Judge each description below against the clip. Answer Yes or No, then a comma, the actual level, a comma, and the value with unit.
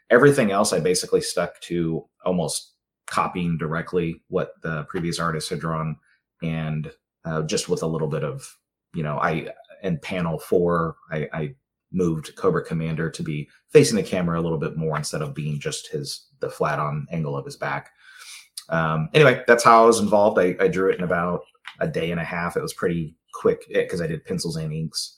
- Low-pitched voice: Yes, very low, 85 Hz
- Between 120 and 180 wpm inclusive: No, average, 195 wpm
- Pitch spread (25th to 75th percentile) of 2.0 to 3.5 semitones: Yes, narrow, 2.4 semitones